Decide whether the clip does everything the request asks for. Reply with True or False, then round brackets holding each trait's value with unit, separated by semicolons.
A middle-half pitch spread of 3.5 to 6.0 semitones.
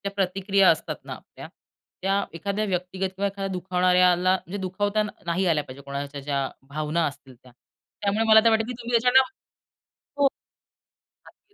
True (3.9 semitones)